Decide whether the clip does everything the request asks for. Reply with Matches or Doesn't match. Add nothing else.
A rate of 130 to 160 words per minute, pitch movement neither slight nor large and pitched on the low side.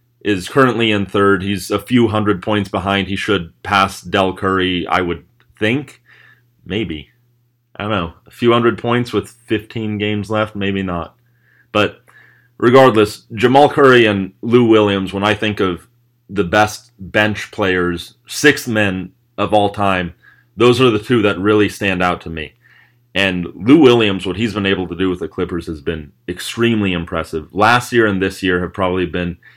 Doesn't match